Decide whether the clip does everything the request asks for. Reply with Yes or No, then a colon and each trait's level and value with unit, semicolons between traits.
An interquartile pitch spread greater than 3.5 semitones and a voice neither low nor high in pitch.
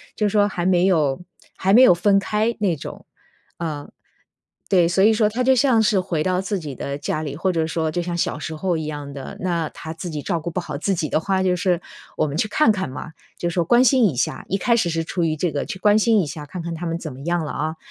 Yes: average, 3.9 semitones; medium, 175 Hz